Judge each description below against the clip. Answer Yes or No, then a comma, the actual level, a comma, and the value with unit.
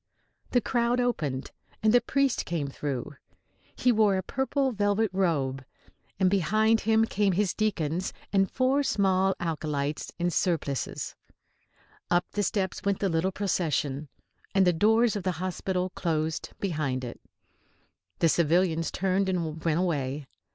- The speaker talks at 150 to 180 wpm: No, average, 140 wpm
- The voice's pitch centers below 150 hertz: No, medium, 185 Hz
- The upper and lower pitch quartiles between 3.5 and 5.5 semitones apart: Yes, average, 4.7 semitones